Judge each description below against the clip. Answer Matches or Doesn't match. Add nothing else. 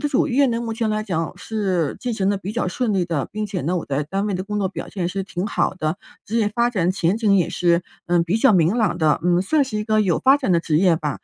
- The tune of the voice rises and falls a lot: Doesn't match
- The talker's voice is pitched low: Doesn't match